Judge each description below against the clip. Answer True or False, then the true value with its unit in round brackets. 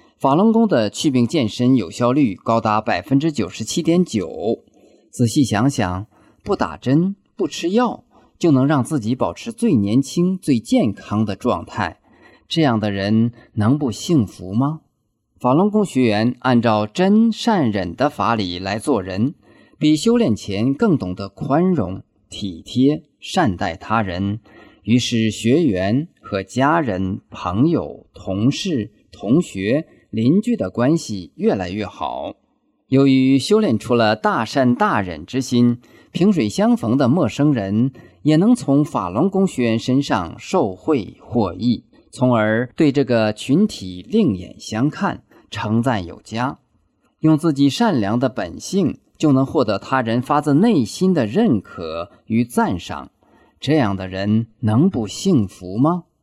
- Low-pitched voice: True (125 Hz)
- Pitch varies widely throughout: True (6.2 semitones)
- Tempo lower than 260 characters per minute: True (205 characters per minute)